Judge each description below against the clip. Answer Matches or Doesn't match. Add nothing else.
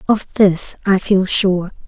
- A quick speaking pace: Doesn't match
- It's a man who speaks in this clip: Doesn't match